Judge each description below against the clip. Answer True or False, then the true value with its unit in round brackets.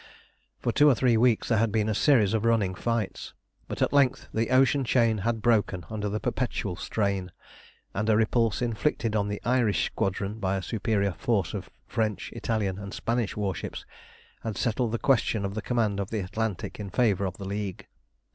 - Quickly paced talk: False (190 wpm)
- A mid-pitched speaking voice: False (110 Hz)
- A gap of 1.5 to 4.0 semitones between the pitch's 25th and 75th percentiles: True (2.7 semitones)